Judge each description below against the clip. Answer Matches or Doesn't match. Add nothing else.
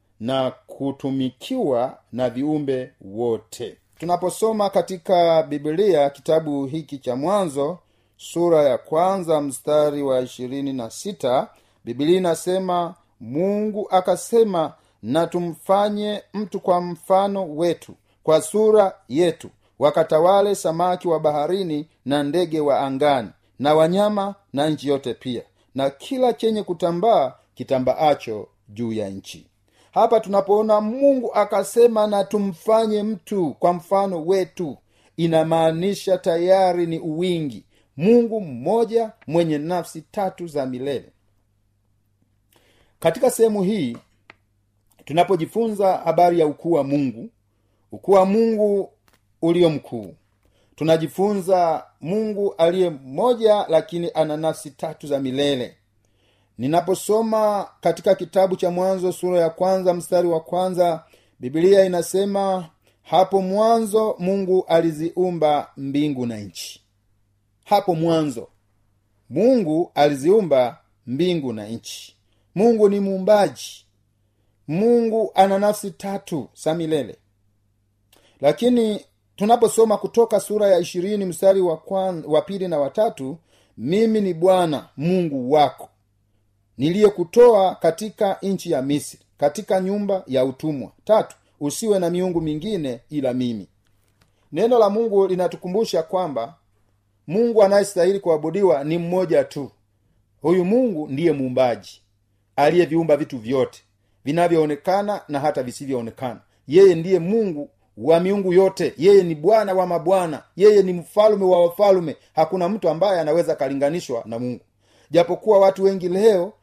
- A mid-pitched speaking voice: Matches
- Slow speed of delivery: Doesn't match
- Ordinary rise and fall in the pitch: Doesn't match